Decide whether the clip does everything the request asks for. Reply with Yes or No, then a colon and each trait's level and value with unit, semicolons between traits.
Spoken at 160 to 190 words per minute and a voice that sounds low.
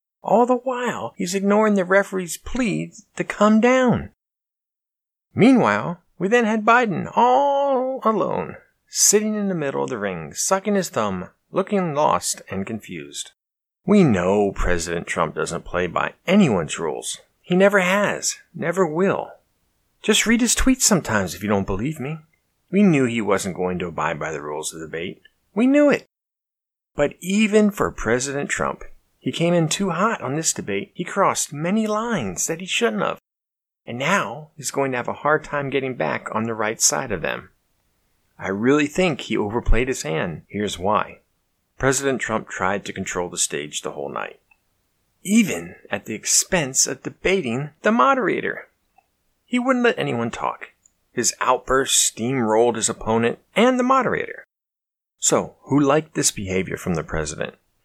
No: average, 165 wpm; medium, 170 Hz